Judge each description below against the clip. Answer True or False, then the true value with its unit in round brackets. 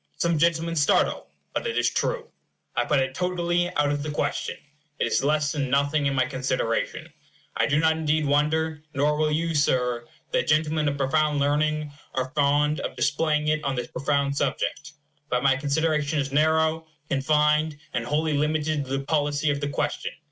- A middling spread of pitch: False (1.8 semitones)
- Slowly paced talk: False (180 wpm)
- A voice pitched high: False (150 Hz)